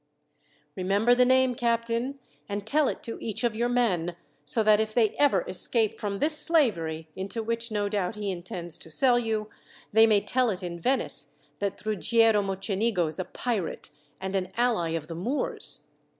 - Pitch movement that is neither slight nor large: Yes, average, 4.0 semitones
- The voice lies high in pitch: Yes, high, 215 Hz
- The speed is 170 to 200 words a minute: Yes, average, 180 wpm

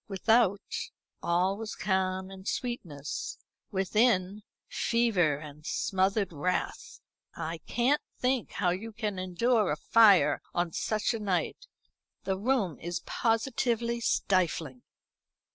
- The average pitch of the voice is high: Yes, high, 195 Hz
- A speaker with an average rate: No, slow, 110 wpm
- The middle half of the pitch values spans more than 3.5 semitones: Yes, average, 4.2 semitones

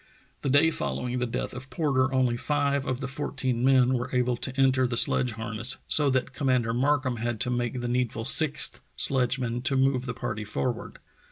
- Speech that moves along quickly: No, average, 190 wpm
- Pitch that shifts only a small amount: Yes, narrow, 1.8 semitones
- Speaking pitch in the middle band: No, low, 125 Hz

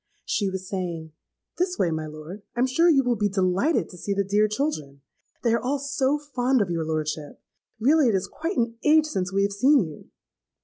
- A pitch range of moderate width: No, wide, 7.1 semitones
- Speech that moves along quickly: Yes, fast, 215 wpm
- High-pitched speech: Yes, high, 210 Hz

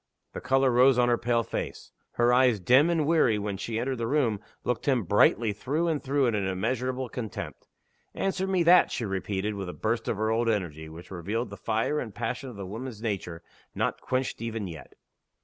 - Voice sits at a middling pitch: No, low, 115 Hz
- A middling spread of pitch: Yes, average, 4.0 semitones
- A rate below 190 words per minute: No, average, 200 wpm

